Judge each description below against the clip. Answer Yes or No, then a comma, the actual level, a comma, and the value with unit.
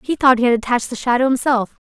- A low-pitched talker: No, high, 245 Hz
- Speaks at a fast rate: Yes, fast, 255 wpm